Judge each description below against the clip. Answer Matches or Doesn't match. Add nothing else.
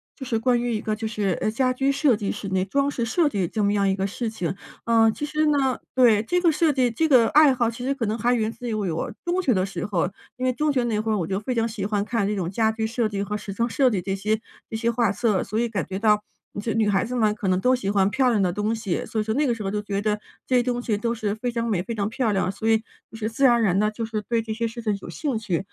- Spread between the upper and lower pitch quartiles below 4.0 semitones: Matches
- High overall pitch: Matches